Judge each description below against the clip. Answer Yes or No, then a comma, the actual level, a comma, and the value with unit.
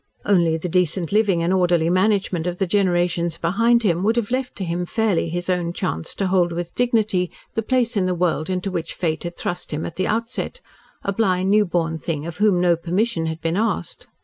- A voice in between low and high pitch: Yes, medium, 180 Hz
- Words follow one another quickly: Yes, fast, 210 wpm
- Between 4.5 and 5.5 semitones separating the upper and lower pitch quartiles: No, average, 3.3 semitones